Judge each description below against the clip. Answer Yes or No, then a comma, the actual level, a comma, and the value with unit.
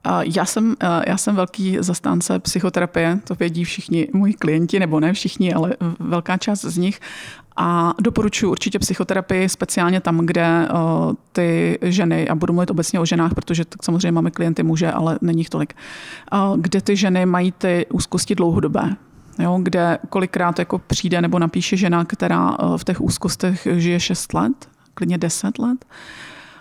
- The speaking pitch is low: No, medium, 180 Hz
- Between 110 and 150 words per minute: No, average, 160 wpm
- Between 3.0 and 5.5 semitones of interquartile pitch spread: No, narrow, 2.4 semitones